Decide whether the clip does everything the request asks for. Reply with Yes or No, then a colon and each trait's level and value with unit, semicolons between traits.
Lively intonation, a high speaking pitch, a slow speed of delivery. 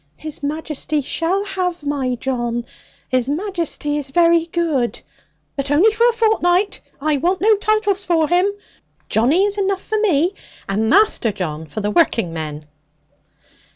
No: wide, 7.1 semitones; very high, 320 Hz; average, 150 wpm